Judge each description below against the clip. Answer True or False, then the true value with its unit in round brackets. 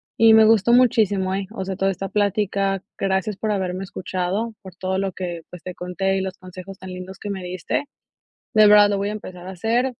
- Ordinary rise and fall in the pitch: False (2.1 semitones)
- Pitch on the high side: True (195 Hz)